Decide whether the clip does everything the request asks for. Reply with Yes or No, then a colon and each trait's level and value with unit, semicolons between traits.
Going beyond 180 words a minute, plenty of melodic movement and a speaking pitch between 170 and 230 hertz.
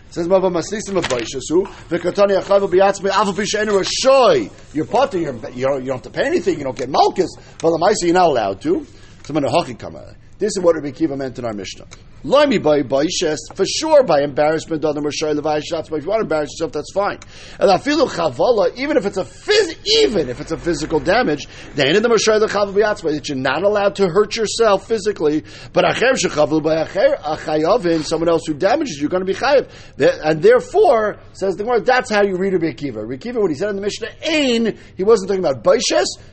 Yes: fast, 205 wpm; wide, 6.1 semitones; medium, 185 Hz